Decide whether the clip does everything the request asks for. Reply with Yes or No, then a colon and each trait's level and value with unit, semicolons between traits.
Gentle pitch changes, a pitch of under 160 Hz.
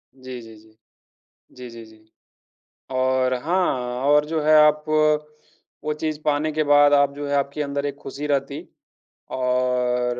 No: average, 3.1 semitones; medium, 140 Hz